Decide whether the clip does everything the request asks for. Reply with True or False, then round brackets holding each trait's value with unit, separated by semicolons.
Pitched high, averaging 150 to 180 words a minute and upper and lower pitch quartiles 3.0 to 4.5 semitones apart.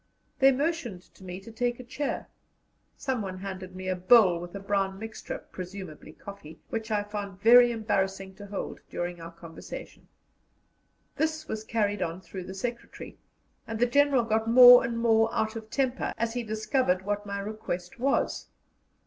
True (215 Hz; 165 wpm; 3.9 semitones)